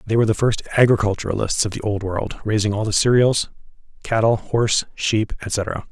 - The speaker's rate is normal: Yes, average, 175 wpm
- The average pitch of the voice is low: Yes, low, 110 Hz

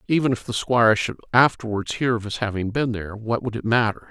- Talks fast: Yes, fast, 235 wpm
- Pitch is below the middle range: Yes, low, 115 Hz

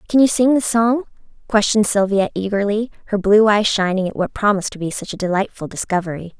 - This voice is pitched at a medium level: No, high, 205 Hz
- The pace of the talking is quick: No, average, 195 wpm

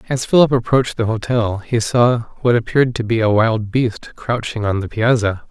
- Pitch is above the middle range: No, low, 115 Hz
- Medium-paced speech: Yes, average, 195 wpm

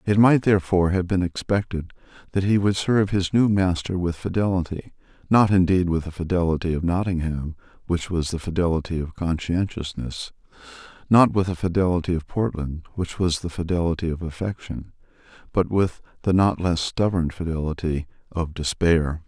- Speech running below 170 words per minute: Yes, average, 155 wpm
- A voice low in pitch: Yes, very low, 90 Hz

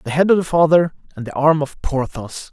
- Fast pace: Yes, fast, 240 wpm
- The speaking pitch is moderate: Yes, medium, 150 Hz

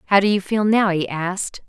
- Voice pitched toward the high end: Yes, high, 195 Hz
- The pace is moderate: No, fast, 250 wpm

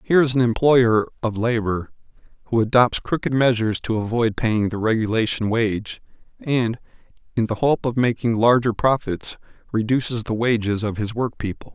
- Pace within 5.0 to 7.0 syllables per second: Yes, 5.1 syllables/s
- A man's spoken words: Yes, male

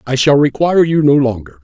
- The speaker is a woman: No, male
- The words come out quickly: Yes, fast, 220 wpm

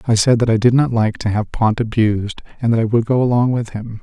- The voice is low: Yes, low, 115 Hz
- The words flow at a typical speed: No, fast, 285 wpm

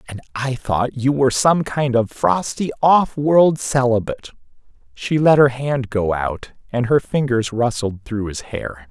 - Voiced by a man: Yes, male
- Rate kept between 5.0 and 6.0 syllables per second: No, 4.1 syllables/s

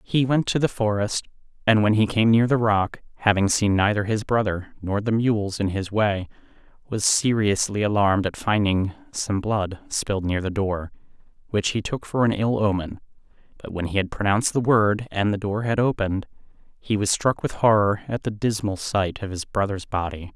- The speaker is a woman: No, male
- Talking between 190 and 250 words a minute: Yes, average, 195 wpm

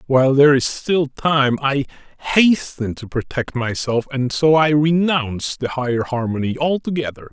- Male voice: Yes, male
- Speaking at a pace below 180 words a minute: Yes, average, 150 wpm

